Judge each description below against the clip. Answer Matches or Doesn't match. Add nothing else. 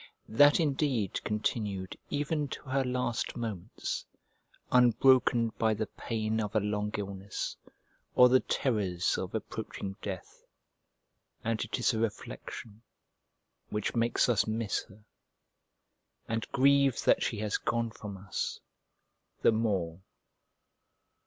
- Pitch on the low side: Matches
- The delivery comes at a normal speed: Doesn't match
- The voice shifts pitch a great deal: Doesn't match